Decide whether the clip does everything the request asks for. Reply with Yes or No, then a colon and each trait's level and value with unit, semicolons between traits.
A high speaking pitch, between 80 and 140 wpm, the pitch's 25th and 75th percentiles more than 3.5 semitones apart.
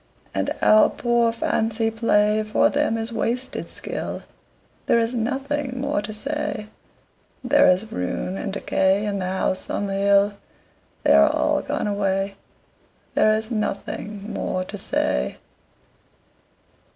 No: high, 215 Hz; slow, 135 wpm; average, 2.7 semitones